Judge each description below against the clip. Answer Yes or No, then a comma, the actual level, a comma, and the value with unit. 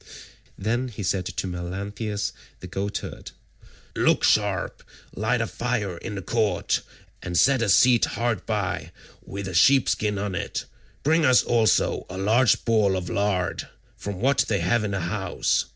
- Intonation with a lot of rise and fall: No, average, 3.6 semitones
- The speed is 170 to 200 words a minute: No, average, 160 wpm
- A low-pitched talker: Yes, low, 105 Hz